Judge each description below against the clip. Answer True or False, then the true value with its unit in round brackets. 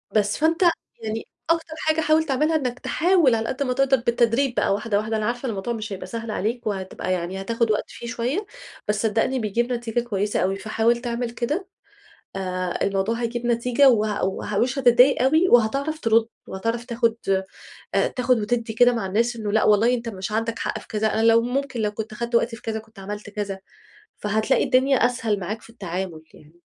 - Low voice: False (230 Hz)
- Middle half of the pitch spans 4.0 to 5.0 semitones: False (3.0 semitones)